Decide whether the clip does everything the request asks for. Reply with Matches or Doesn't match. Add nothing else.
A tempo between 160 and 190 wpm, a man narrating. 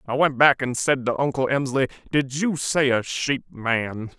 Doesn't match